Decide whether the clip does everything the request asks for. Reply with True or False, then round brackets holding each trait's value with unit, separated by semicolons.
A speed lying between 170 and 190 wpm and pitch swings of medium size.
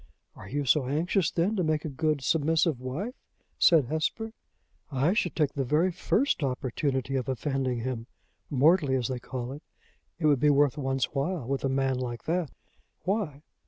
True (175 wpm; 3.7 semitones)